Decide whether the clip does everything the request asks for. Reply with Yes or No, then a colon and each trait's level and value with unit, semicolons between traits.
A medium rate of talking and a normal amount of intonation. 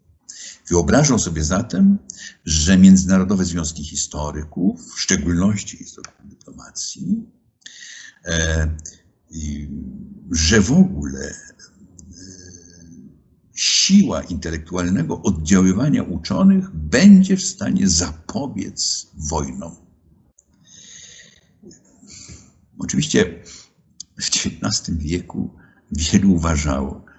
No: slow, 65 wpm; average, 4.1 semitones